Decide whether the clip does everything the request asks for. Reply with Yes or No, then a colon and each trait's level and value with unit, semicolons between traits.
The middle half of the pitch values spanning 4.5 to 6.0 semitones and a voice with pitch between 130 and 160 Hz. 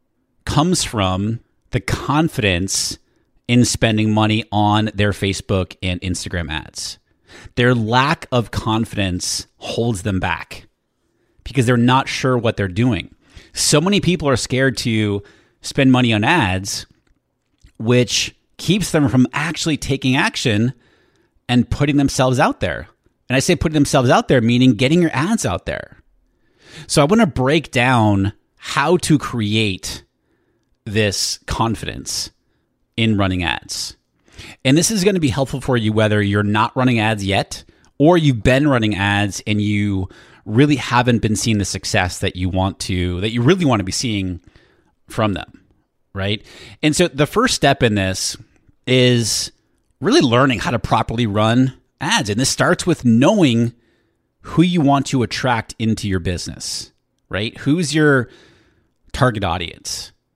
No: average, 4.9 semitones; low, 115 Hz